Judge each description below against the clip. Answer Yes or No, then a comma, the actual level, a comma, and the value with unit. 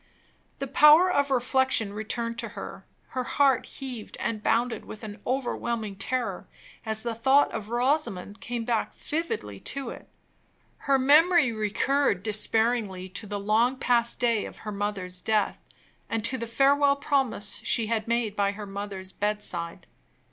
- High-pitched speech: Yes, high, 230 Hz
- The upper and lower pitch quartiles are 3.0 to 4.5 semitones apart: Yes, average, 4.1 semitones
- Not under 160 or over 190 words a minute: No, average, 150 wpm